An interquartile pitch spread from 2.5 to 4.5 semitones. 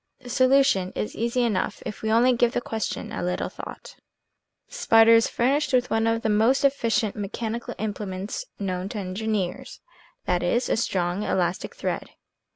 Yes: average, 3.8 semitones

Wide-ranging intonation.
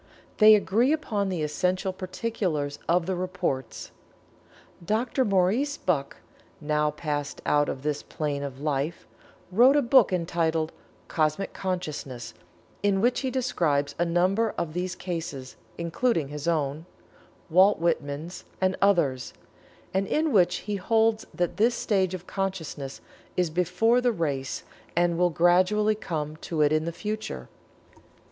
No: average, 5.0 semitones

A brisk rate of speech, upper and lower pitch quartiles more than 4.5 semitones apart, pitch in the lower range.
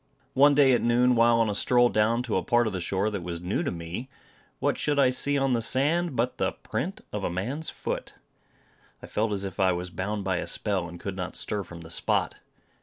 Yes: fast, 240 wpm; average, 5.2 semitones; low, 110 Hz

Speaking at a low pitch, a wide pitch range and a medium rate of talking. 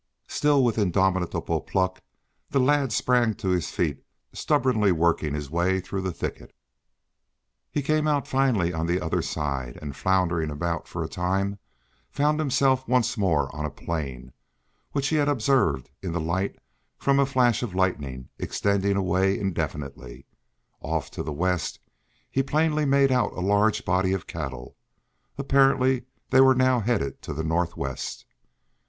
Yes: very low, 95 Hz; wide, 7.8 semitones; average, 155 wpm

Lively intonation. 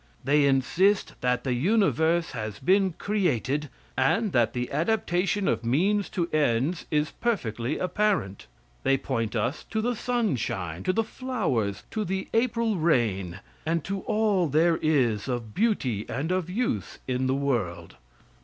Yes: wide, 8.4 semitones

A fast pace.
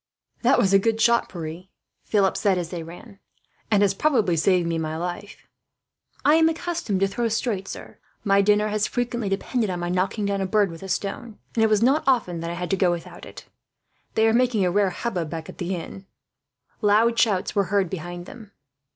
Yes: fast, 210 wpm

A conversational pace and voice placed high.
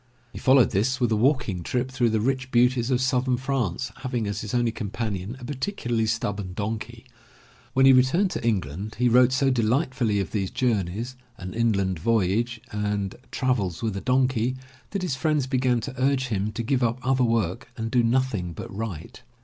No: average, 185 wpm; low, 120 Hz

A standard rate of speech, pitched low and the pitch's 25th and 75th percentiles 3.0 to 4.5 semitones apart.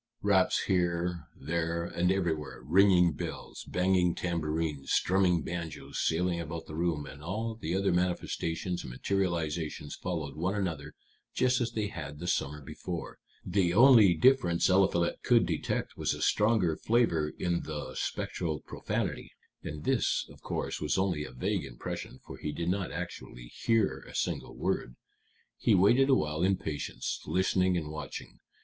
Yes: average, 150 wpm; very low, 85 Hz; average, 3.6 semitones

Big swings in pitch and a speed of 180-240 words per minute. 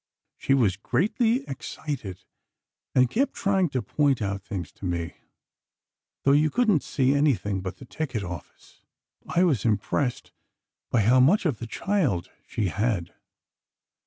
No: wide, 7.5 semitones; average, 140 wpm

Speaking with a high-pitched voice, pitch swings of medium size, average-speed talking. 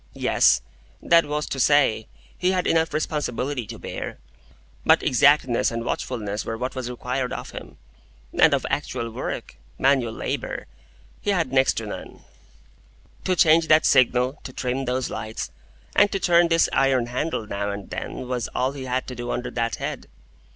No: low, 130 Hz; average, 3.9 semitones; average, 165 wpm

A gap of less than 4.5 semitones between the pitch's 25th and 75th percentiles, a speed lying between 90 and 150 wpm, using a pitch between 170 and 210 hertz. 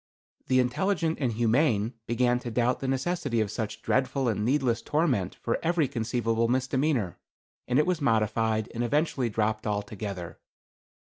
No: average, 3.5 semitones; average, 145 wpm; low, 120 Hz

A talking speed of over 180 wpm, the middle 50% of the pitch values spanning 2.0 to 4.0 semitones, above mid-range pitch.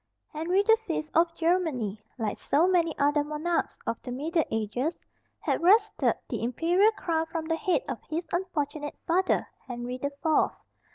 No: average, 160 wpm; average, 3.6 semitones; very high, 320 Hz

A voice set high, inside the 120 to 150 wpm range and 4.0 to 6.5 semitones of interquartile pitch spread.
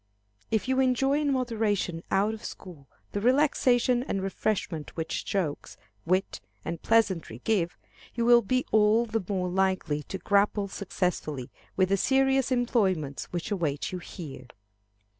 Yes: high, 200 Hz; average, 140 wpm; average, 5.1 semitones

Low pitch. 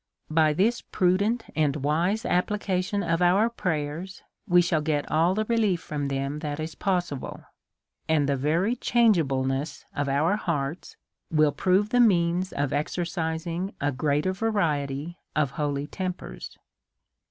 No: medium, 165 Hz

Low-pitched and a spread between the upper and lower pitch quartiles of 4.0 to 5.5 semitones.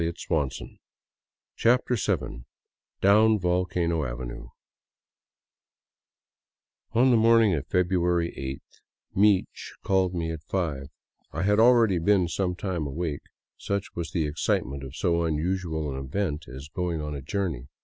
Yes: very low, 85 Hz; average, 4.5 semitones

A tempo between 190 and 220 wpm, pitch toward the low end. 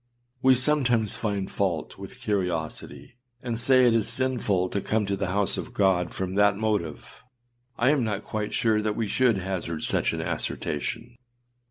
No: average, 170 wpm; low, 105 Hz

